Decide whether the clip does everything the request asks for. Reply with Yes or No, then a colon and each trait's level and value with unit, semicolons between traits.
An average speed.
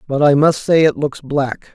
No: fast, 240 wpm